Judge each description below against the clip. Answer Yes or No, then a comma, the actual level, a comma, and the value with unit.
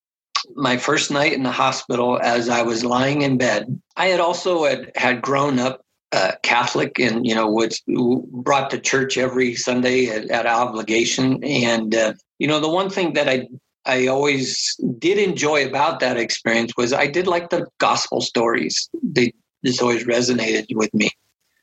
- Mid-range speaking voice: No, low, 130 Hz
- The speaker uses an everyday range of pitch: Yes, average, 3.3 semitones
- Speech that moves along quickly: No, average, 170 wpm